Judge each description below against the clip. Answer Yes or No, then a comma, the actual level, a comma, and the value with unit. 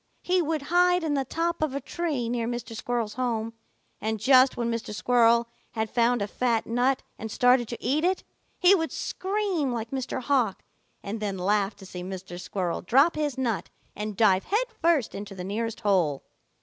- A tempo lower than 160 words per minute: No, average, 185 wpm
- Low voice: No, high, 240 Hz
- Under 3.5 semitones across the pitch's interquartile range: No, wide, 5.5 semitones